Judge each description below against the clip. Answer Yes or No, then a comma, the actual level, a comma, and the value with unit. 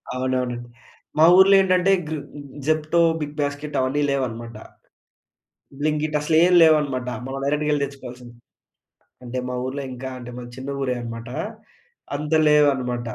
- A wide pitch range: No, average, 3.1 semitones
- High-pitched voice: No, medium, 140 Hz